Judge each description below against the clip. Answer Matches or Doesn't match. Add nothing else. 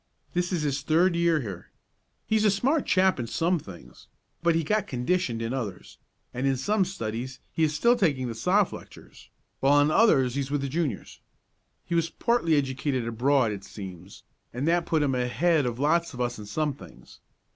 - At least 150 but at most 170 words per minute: Doesn't match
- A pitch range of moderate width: Doesn't match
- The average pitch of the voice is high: Doesn't match